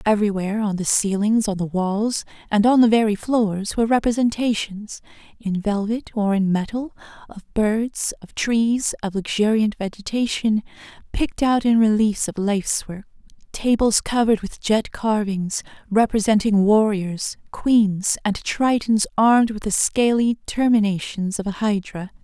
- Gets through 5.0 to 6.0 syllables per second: No, 4.5 syllables/s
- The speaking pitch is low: No, high, 215 Hz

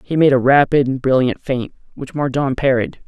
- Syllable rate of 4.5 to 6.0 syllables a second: Yes, 5.1 syllables/s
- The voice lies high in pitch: No, low, 135 Hz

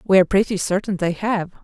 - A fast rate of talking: Yes, fast, 220 wpm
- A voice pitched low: No, high, 190 Hz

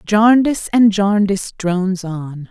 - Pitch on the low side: No, high, 200 Hz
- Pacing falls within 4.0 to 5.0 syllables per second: Yes, 4.2 syllables/s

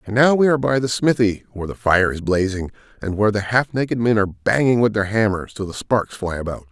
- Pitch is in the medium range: No, low, 110 Hz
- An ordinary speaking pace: No, fast, 250 wpm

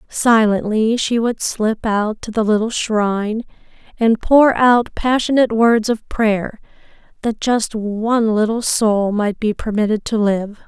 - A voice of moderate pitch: No, high, 220 Hz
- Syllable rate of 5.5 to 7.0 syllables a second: No, 4.0 syllables/s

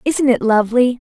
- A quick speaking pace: No, average, 155 wpm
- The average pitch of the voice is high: Yes, high, 245 Hz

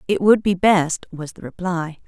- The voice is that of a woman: Yes, female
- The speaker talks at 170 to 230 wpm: Yes, average, 200 wpm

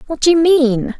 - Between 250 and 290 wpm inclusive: No, fast, 240 wpm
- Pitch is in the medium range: No, very high, 295 Hz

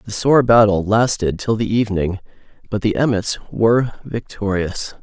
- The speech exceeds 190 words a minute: No, average, 145 wpm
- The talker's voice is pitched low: Yes, low, 105 Hz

